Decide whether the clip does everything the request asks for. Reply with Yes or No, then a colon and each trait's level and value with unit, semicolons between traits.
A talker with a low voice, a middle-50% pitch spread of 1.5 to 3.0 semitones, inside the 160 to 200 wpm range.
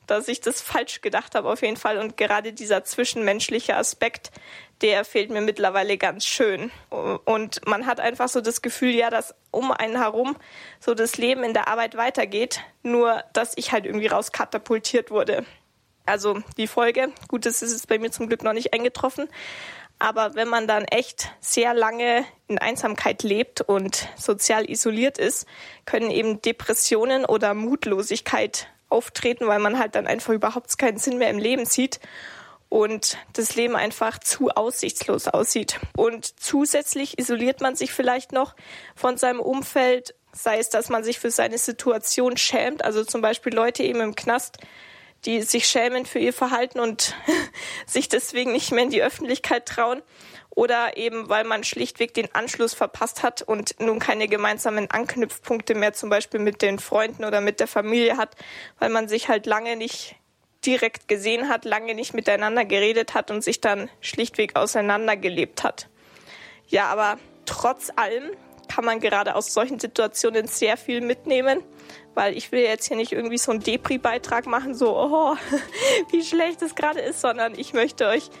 No: high, 230 Hz; narrow, 2.5 semitones; average, 170 wpm